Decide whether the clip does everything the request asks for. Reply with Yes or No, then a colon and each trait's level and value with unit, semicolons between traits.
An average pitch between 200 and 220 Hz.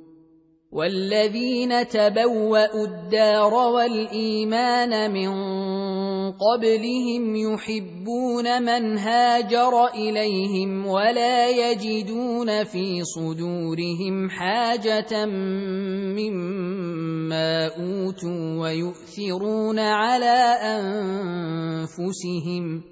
Yes: high, 210 Hz